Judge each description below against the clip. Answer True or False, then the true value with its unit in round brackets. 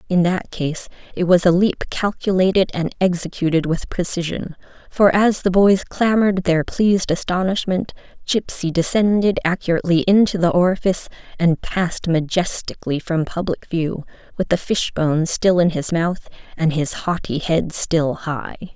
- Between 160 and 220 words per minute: False (145 wpm)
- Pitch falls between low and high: True (175 Hz)